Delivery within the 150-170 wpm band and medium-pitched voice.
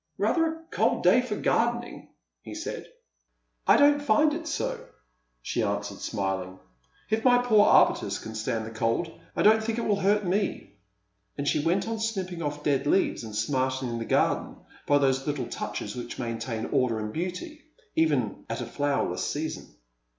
No: average, 180 wpm; medium, 150 Hz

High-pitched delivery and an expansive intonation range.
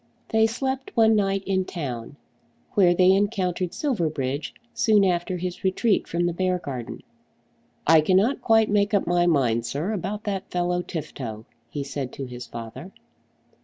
No: medium, 180 Hz; wide, 5.9 semitones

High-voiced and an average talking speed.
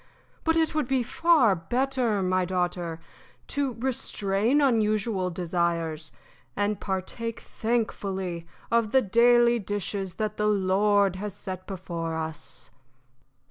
No: high, 205 Hz; slow, 115 wpm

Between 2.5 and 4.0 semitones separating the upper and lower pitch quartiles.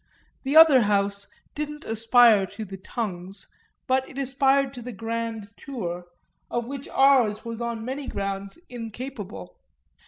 No: average, 4.8 semitones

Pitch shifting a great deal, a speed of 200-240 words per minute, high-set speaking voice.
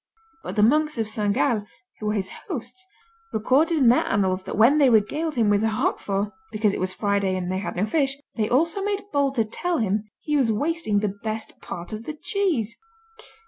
Yes: wide, 6.2 semitones; fast, 205 wpm; high, 225 Hz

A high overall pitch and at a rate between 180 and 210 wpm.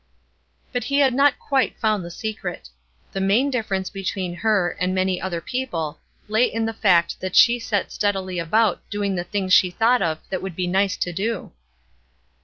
Yes: high, 195 Hz; average, 185 wpm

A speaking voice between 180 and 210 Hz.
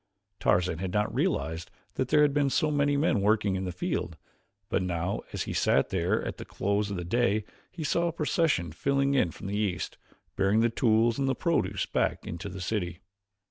No: low, 105 Hz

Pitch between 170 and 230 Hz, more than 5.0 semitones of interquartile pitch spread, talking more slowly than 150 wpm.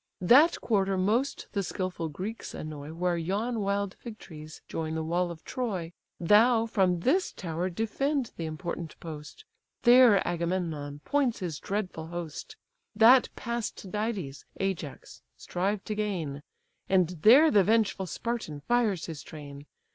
Yes: high, 190 Hz; wide, 5.5 semitones; average, 140 wpm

